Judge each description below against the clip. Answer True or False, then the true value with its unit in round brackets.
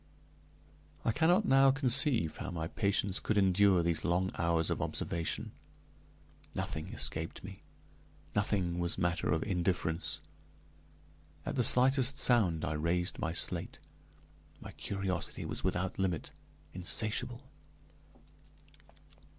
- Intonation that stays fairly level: False (4.7 semitones)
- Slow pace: True (110 wpm)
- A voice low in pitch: True (95 Hz)